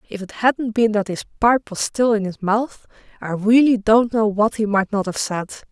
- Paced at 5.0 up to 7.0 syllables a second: No, 4.7 syllables/s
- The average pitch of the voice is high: Yes, high, 215 Hz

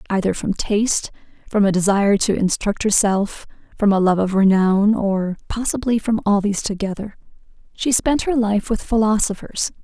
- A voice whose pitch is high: Yes, high, 205 Hz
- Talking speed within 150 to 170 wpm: Yes, average, 160 wpm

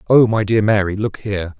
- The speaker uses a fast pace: Yes, fast, 225 wpm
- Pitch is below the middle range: Yes, low, 105 Hz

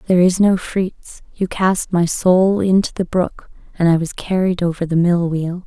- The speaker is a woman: Yes, female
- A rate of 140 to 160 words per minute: No, average, 200 wpm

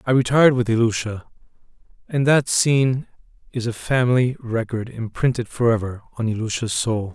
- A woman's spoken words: No, male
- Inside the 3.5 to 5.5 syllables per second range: Yes, 5.3 syllables/s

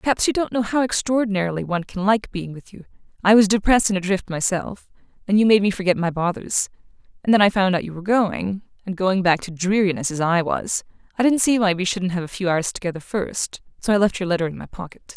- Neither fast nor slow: No, fast, 225 wpm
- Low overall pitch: No, high, 195 Hz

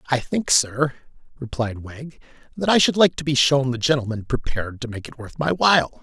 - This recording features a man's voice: Yes, male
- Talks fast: Yes, fast, 210 wpm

